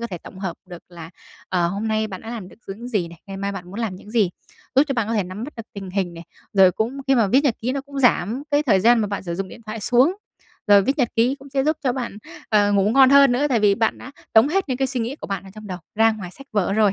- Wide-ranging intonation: No, average, 4.8 semitones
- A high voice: Yes, high, 220 Hz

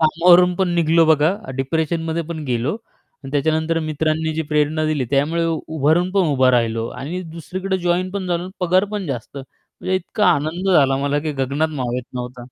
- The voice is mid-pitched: Yes, medium, 160 Hz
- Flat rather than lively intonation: No, average, 3.8 semitones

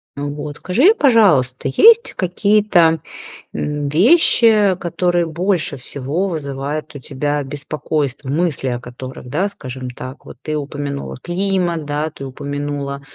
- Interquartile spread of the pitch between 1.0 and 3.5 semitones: No, average, 4.5 semitones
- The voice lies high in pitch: No, medium, 150 Hz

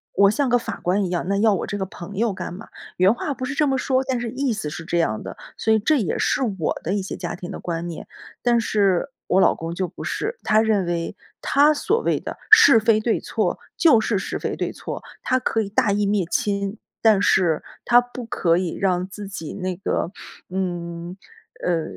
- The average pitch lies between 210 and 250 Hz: No, high, 200 Hz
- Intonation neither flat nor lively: Yes, average, 4.8 semitones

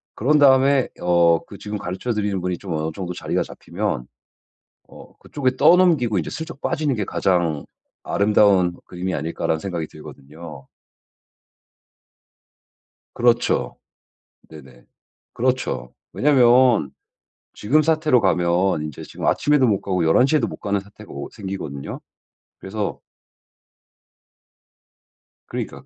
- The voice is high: No, low, 100 Hz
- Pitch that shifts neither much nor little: No, wide, 7.1 semitones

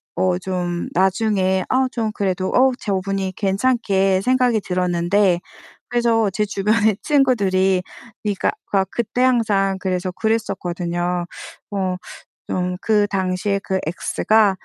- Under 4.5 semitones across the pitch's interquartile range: Yes, average, 2.9 semitones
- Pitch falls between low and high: No, high, 195 Hz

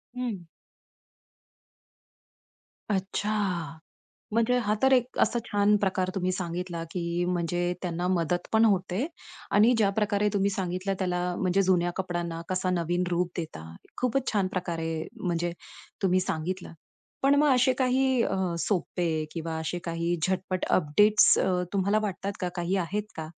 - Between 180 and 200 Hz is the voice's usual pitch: Yes, medium, 185 Hz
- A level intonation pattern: No, average, 3.0 semitones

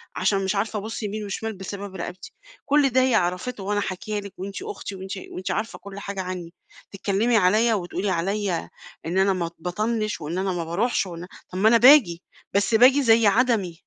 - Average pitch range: Yes, average, 3.3 semitones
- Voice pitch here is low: No, high, 200 Hz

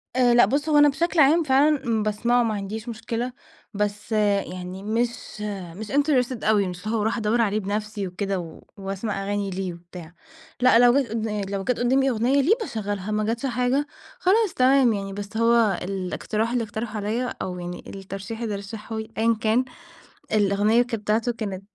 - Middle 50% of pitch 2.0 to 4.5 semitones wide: Yes, average, 3.4 semitones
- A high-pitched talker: Yes, high, 220 Hz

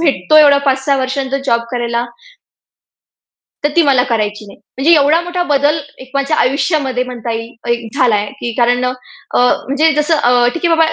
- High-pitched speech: Yes, very high, 265 Hz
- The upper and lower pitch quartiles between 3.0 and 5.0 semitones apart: Yes, average, 3.8 semitones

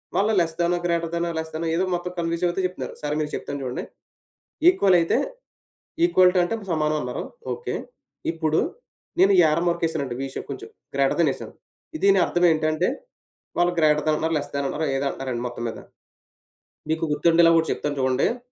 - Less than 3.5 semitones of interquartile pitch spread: Yes, average, 2.8 semitones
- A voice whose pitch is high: No, medium, 165 Hz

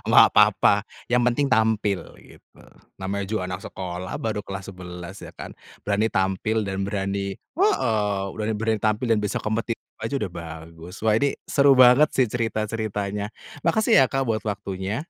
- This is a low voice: Yes, low, 105 Hz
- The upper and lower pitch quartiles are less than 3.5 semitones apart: Yes, average, 2.8 semitones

